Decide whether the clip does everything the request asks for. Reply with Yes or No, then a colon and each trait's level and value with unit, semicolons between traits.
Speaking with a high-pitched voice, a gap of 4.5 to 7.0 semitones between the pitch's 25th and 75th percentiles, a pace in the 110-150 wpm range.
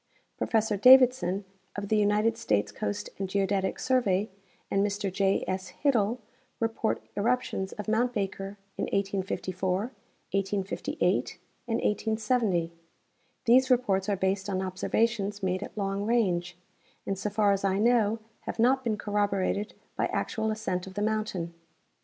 No: high, 205 Hz; narrow, 2.5 semitones; average, 140 wpm